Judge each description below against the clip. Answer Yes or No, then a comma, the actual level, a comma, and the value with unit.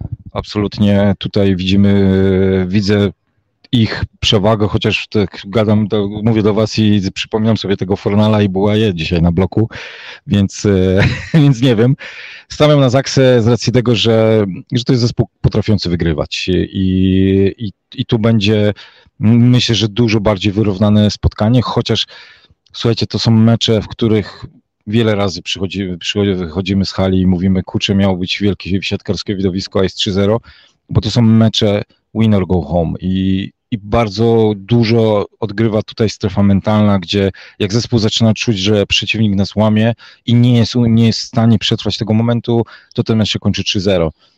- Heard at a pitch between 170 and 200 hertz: No, low, 105 Hz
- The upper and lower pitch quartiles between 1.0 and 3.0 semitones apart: Yes, narrow, 2.6 semitones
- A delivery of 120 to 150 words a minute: No, fast, 160 wpm